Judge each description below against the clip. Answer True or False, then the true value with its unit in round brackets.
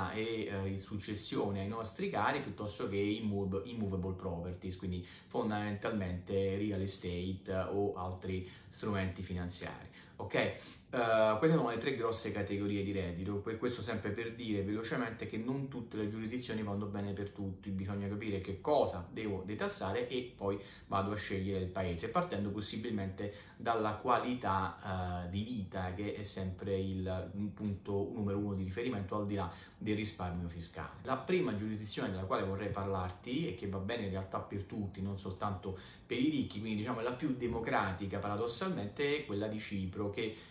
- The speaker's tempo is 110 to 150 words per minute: False (165 wpm)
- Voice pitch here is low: True (100 Hz)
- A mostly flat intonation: True (2.2 semitones)